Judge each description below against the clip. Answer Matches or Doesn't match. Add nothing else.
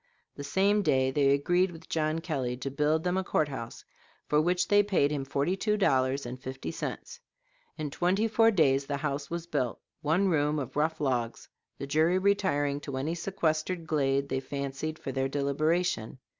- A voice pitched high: Doesn't match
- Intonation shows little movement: Doesn't match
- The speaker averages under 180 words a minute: Doesn't match